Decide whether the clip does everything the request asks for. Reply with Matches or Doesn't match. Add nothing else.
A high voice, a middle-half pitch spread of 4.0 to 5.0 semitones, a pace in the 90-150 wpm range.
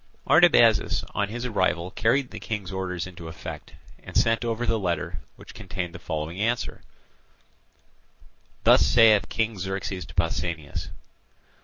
Doesn't match